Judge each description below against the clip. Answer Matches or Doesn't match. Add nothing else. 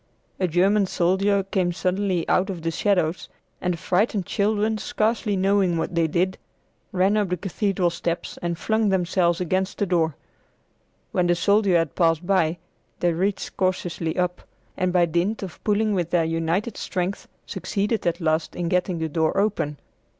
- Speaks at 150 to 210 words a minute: Matches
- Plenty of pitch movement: Doesn't match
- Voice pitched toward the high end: Doesn't match